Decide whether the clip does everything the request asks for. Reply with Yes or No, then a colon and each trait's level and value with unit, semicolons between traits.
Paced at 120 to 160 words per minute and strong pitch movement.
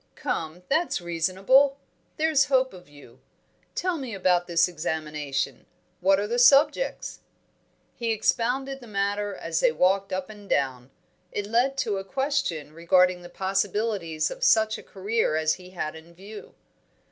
Yes: average, 150 wpm; wide, 6.0 semitones